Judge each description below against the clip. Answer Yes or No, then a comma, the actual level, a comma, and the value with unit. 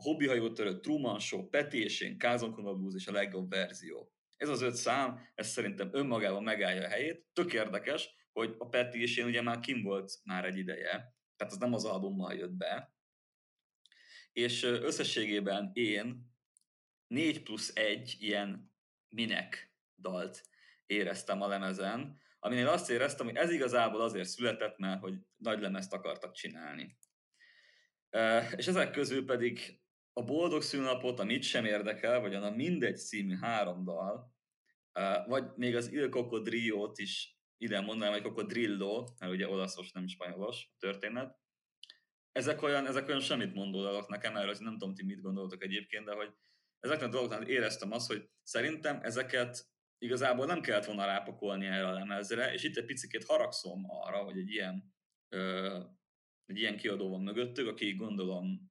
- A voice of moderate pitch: No, low, 105 Hz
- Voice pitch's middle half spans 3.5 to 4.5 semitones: Yes, average, 4.1 semitones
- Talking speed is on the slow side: No, fast, 155 wpm